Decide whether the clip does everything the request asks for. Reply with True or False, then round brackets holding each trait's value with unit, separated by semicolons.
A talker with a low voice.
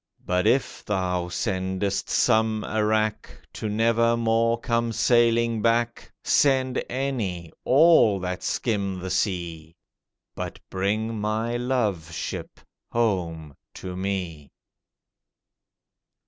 True (110 Hz)